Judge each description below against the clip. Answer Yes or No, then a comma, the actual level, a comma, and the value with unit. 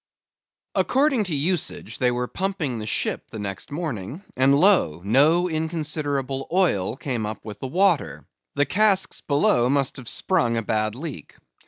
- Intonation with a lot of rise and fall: Yes, wide, 6.6 semitones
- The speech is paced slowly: No, average, 150 wpm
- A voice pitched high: No, medium, 140 Hz